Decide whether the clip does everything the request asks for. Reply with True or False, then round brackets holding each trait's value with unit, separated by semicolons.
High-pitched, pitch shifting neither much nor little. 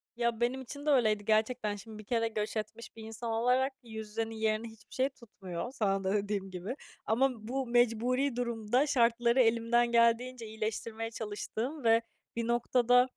False (230 Hz; 2.1 semitones)